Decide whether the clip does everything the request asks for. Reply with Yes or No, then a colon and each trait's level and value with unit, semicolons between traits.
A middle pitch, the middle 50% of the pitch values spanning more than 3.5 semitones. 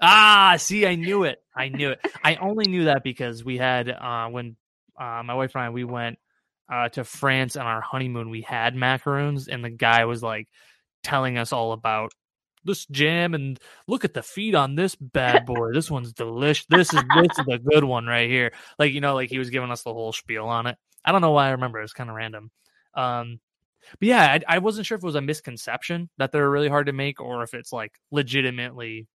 No: low, 130 Hz; average, 4.0 semitones